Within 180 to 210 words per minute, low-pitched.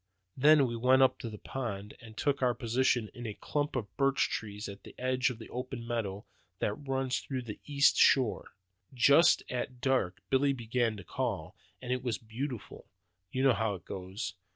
Yes: average, 190 wpm; low, 125 Hz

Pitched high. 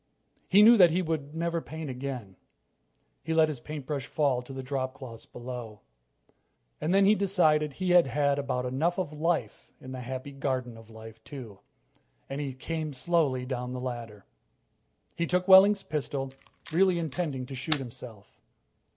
No: medium, 140 Hz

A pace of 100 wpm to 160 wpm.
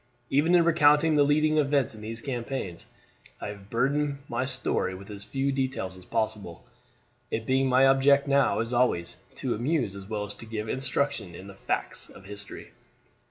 No: average, 180 wpm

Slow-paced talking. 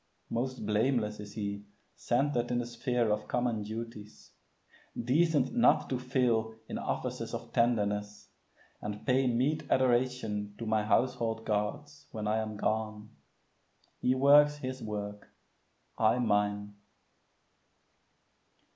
Yes: slow, 120 wpm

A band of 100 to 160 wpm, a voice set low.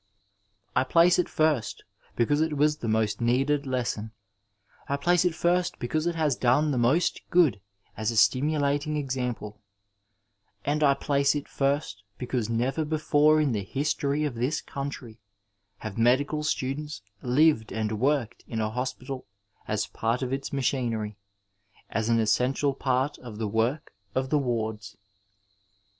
Yes: average, 150 wpm; low, 130 Hz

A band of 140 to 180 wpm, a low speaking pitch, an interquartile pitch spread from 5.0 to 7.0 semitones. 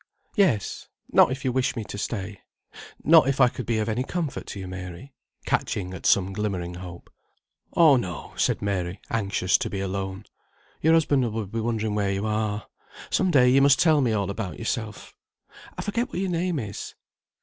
No: average, 190 wpm; low, 110 Hz; wide, 5.6 semitones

